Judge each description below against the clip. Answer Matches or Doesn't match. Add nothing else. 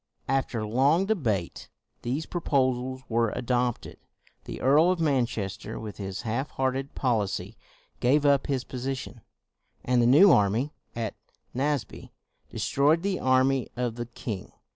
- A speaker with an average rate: Doesn't match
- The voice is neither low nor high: Doesn't match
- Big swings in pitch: Doesn't match